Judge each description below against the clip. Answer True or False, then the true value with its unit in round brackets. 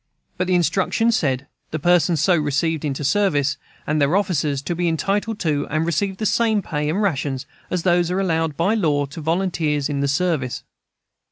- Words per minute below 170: False (180 wpm)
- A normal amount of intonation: True (4.1 semitones)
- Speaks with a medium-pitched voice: True (165 Hz)